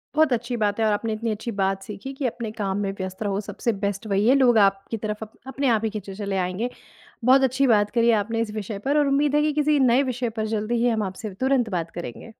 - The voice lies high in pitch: Yes, high, 220 Hz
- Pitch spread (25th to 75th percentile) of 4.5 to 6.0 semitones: No, average, 3.7 semitones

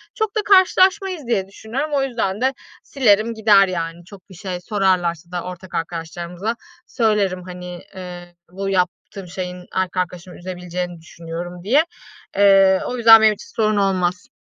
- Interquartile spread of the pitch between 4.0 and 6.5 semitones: No, average, 3.6 semitones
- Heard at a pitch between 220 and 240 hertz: No, high, 190 Hz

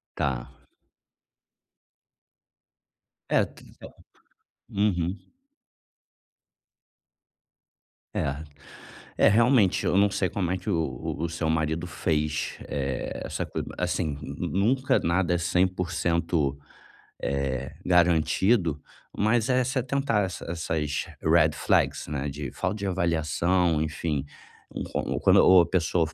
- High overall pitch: No, very low, 85 Hz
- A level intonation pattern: No, average, 3.8 semitones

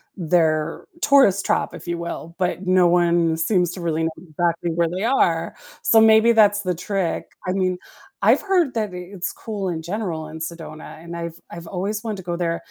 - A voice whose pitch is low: No, medium, 175 Hz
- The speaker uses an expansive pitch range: No, average, 3.2 semitones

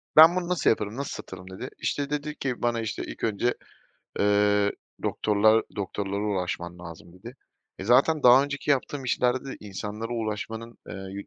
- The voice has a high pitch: No, low, 110 Hz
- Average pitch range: Yes, average, 4.6 semitones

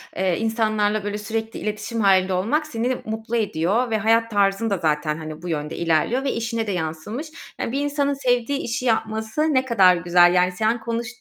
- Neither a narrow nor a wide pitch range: Yes, average, 4.3 semitones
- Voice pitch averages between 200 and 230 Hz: Yes, high, 220 Hz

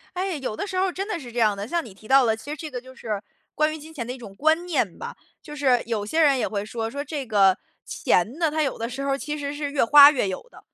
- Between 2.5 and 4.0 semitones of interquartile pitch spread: No, average, 5.3 semitones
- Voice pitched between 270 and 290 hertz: Yes, very high, 275 Hz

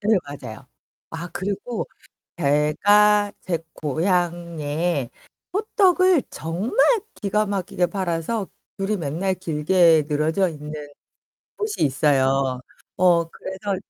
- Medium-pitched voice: Yes, medium, 175 Hz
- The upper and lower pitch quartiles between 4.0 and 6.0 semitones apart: Yes, average, 5.3 semitones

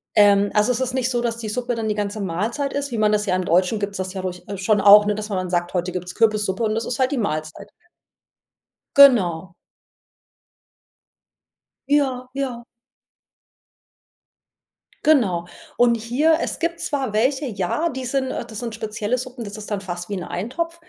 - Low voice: No, high, 215 Hz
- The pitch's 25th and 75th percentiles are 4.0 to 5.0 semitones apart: Yes, average, 4.5 semitones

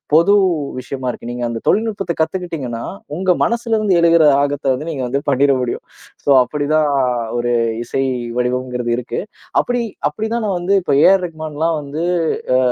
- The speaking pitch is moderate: Yes, medium, 155 Hz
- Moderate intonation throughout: No, wide, 6.3 semitones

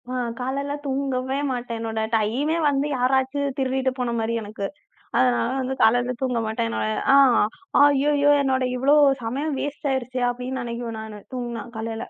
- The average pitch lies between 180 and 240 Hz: No, very high, 255 Hz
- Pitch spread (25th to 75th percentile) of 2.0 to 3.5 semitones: Yes, average, 3.0 semitones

